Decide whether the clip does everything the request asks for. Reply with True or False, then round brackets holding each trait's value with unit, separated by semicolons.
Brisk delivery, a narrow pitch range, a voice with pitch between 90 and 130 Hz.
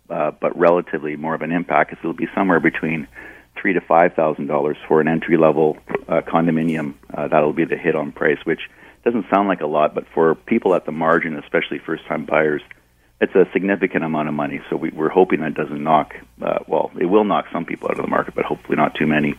False (230 wpm; 1.5 semitones; 80 Hz)